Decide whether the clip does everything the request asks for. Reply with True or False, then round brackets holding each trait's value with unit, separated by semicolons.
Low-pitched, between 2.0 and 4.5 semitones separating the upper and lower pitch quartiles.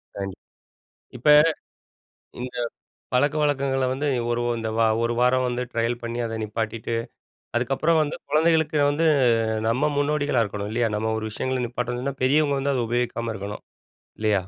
True (125 Hz; 3.8 semitones)